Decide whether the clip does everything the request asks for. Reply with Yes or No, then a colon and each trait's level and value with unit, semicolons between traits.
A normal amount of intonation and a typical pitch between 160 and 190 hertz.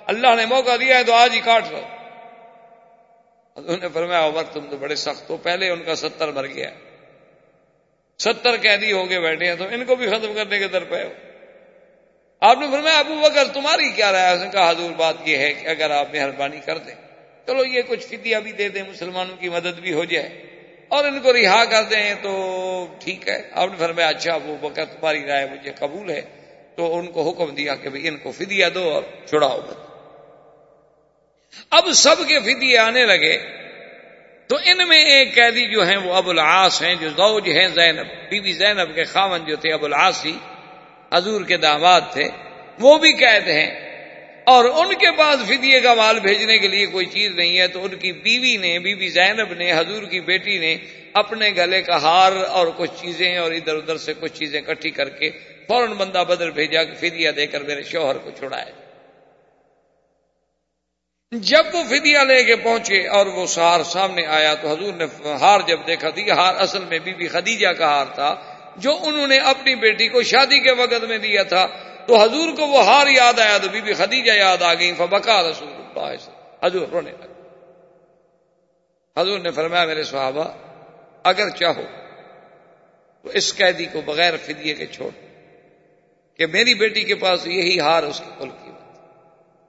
No: wide, 5.8 semitones; medium, 185 Hz